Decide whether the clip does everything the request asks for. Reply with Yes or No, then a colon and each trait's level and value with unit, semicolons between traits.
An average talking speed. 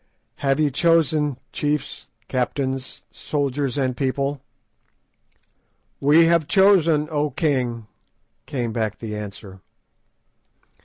No: slow, 95 wpm